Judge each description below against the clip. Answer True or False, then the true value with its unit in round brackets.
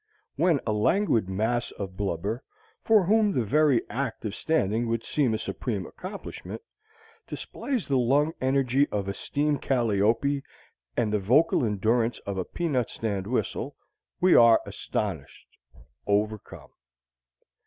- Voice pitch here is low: True (120 Hz)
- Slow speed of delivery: True (130 wpm)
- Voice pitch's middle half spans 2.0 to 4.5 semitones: False (5.4 semitones)